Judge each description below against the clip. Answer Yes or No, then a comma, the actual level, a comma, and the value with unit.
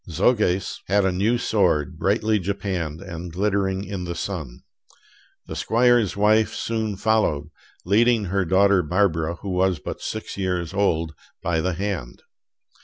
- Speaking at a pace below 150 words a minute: Yes, average, 140 wpm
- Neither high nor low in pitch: No, very low, 95 Hz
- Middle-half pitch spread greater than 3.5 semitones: No, average, 3.1 semitones